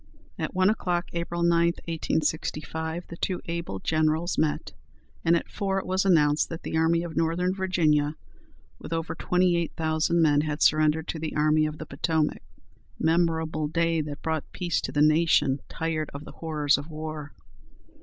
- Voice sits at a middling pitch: Yes, medium, 160 Hz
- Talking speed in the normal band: Yes, average, 170 wpm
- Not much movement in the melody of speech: Yes, narrow, 1.7 semitones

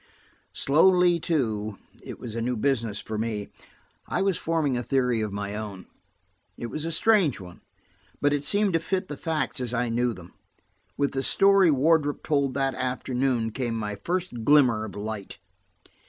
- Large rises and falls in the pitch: Yes, wide, 5.8 semitones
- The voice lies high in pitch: No, low, 130 Hz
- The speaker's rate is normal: Yes, average, 165 wpm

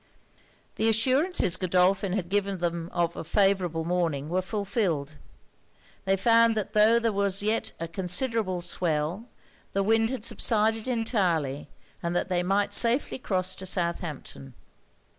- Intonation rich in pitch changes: No, average, 4.3 semitones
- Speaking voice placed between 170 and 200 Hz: Yes, high, 190 Hz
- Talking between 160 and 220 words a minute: No, average, 140 wpm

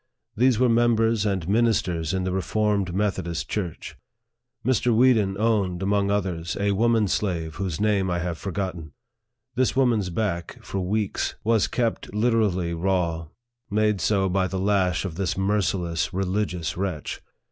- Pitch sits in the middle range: No, very low, 95 Hz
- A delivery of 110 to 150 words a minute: Yes, average, 145 wpm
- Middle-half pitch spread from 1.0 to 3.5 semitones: Yes, average, 3.1 semitones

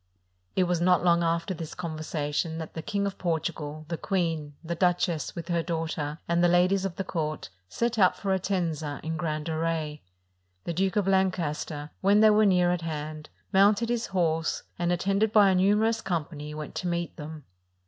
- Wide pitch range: No, average, 3.3 semitones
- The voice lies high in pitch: No, medium, 170 Hz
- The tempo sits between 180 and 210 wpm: Yes, average, 190 wpm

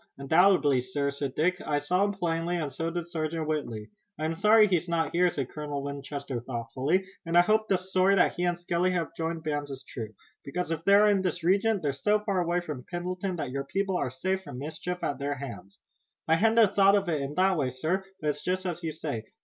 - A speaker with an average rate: No, fast, 230 wpm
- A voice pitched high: No, medium, 165 Hz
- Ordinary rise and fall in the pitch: Yes, average, 4.5 semitones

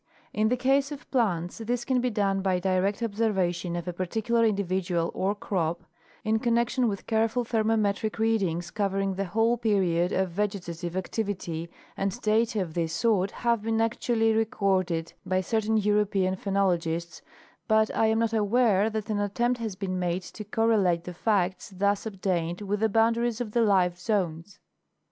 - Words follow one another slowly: No, average, 165 wpm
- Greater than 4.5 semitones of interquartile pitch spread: No, average, 3.4 semitones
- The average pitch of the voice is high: Yes, high, 205 Hz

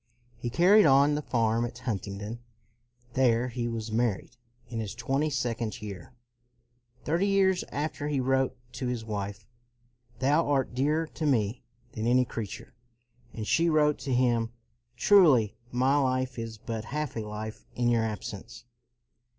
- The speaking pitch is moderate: No, low, 120 Hz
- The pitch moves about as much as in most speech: Yes, average, 3.7 semitones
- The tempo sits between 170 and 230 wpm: No, average, 155 wpm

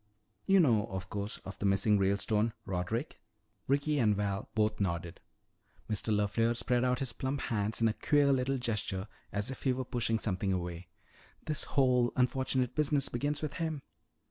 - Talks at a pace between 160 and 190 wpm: Yes, average, 170 wpm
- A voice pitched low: Yes, low, 115 Hz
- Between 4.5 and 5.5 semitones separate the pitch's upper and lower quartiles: Yes, average, 4.8 semitones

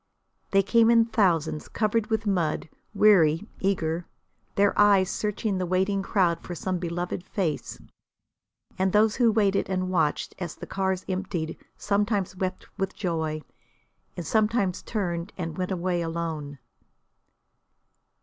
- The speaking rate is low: Yes, slow, 130 wpm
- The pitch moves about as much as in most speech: Yes, average, 3.3 semitones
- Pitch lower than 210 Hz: Yes, medium, 185 Hz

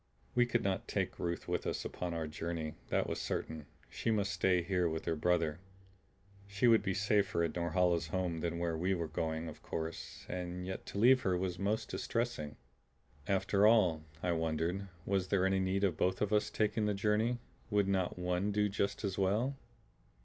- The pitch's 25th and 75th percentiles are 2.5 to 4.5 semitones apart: Yes, average, 3.2 semitones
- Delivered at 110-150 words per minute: No, average, 190 wpm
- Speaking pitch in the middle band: No, very low, 95 Hz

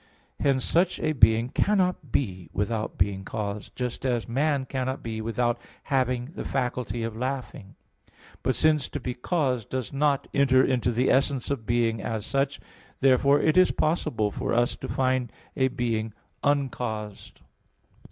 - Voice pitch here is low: Yes, low, 125 Hz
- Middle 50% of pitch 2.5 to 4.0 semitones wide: Yes, average, 3.4 semitones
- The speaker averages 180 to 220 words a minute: No, average, 150 wpm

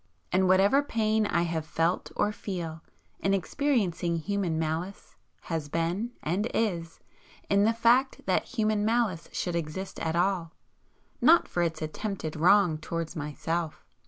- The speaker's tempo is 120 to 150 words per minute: Yes, average, 140 wpm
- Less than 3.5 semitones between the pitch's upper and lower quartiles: No, average, 4.2 semitones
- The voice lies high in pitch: No, medium, 180 Hz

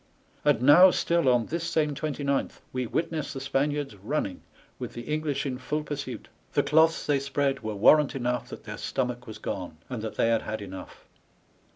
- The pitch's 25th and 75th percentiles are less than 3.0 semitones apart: No, average, 4.1 semitones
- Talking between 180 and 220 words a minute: Yes, average, 185 wpm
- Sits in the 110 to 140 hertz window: Yes, low, 135 Hz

